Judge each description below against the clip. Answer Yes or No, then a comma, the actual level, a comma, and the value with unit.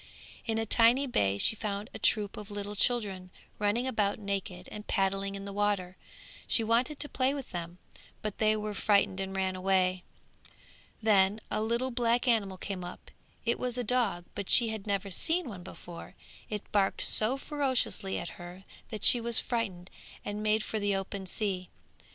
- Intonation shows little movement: No, average, 3.1 semitones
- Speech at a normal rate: Yes, average, 180 wpm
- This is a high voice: Yes, high, 205 Hz